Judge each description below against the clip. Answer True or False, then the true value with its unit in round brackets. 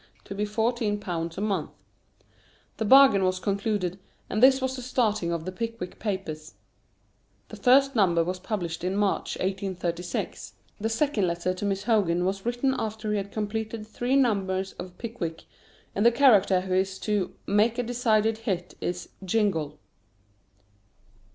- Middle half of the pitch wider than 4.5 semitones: False (3.5 semitones)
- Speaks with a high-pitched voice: True (205 Hz)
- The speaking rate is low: False (155 wpm)